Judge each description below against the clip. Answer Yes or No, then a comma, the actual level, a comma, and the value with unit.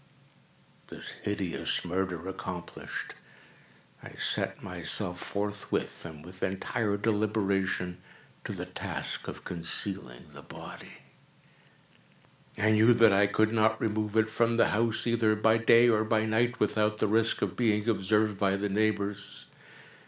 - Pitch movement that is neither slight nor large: No, narrow, 2.3 semitones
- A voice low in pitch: Yes, low, 105 Hz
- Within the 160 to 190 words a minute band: No, slow, 135 wpm